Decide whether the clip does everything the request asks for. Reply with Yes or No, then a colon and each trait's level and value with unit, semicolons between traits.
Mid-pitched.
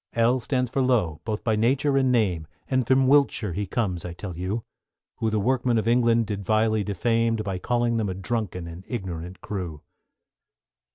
No: low, 110 Hz